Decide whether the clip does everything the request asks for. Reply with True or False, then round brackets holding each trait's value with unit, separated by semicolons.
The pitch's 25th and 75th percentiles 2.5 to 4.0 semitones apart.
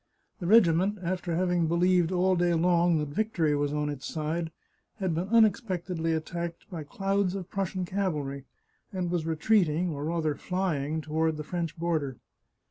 True (2.8 semitones)